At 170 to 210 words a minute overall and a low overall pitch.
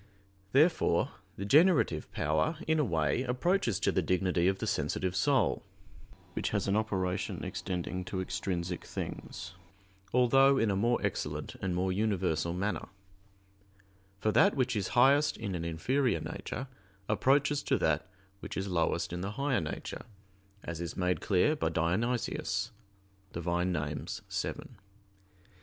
No: average, 140 wpm; very low, 95 Hz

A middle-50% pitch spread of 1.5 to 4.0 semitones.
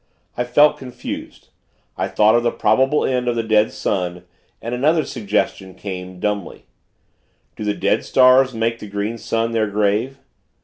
Yes: average, 3.3 semitones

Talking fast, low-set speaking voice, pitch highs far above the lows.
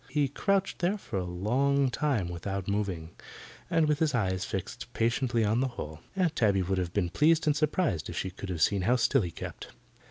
Yes: fast, 210 wpm; low, 110 Hz; wide, 7.5 semitones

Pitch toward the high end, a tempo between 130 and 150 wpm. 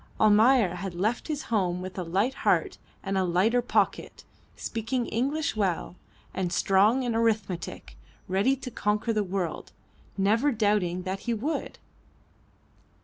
Yes: high, 210 Hz; average, 140 wpm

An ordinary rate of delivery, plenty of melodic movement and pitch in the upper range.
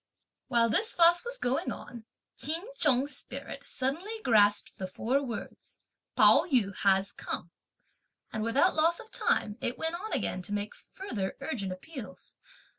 Yes: average, 150 wpm; wide, 8.2 semitones; very high, 250 Hz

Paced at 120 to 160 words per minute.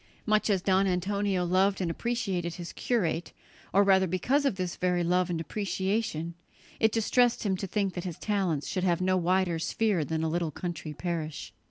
No: average, 185 wpm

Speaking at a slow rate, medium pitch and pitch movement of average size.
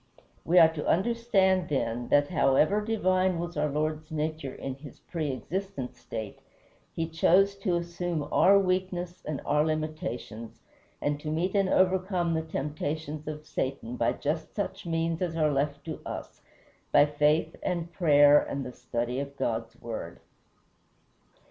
No: average, 150 wpm; medium, 155 Hz; average, 3.8 semitones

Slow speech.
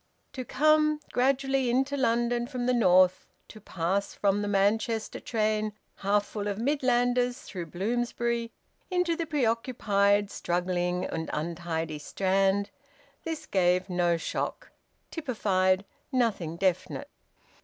Yes: slow, 115 wpm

